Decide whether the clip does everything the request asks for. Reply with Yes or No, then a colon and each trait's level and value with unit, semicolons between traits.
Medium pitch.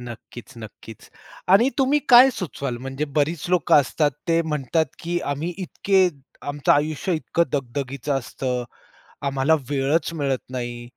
Yes: medium, 145 Hz